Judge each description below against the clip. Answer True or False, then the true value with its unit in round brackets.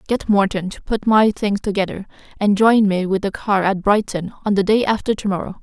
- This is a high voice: True (200 Hz)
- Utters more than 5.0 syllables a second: True (5.4 syllables/s)